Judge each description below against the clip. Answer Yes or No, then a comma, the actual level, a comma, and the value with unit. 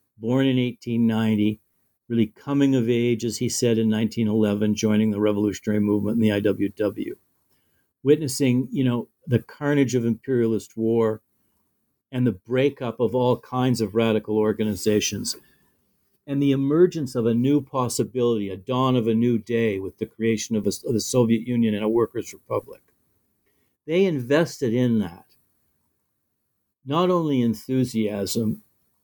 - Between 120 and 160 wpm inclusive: Yes, average, 145 wpm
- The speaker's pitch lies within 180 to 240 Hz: No, low, 115 Hz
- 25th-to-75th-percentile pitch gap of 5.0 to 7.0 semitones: No, average, 3.0 semitones